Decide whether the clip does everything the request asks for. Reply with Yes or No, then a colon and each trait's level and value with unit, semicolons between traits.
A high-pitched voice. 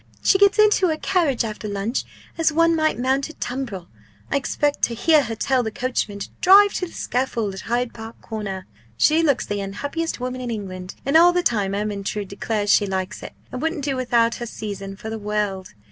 Yes: high, 235 Hz